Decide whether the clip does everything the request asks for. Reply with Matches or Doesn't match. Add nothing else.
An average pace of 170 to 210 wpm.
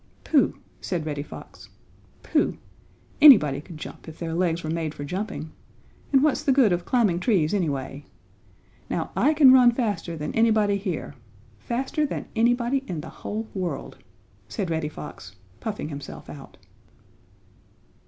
Doesn't match